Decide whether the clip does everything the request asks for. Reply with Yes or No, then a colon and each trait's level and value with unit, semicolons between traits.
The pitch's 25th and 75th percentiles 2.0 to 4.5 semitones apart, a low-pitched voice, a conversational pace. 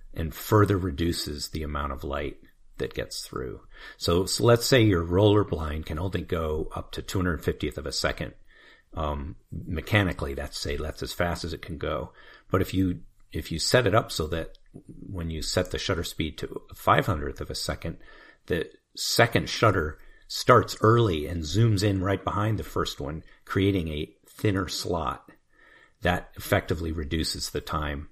Yes: average, 4.2 semitones; very low, 85 Hz; average, 170 wpm